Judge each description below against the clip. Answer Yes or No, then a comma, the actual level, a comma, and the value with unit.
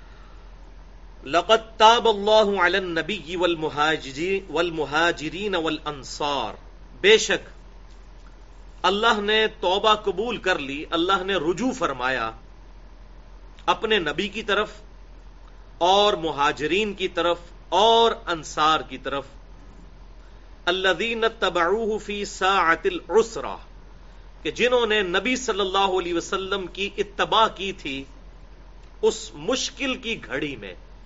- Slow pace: Yes, slow, 100 wpm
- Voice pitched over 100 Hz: Yes, high, 190 Hz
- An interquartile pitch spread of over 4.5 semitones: Yes, average, 5.0 semitones